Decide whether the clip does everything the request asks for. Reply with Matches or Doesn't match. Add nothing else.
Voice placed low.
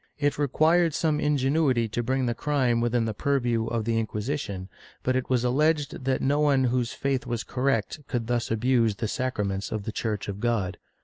Matches